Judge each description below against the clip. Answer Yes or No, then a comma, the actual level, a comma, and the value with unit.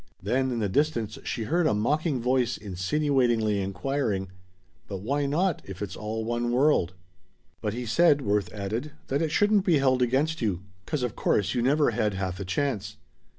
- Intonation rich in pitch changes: Yes, wide, 5.8 semitones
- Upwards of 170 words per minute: Yes, average, 180 wpm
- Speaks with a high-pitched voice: No, low, 120 Hz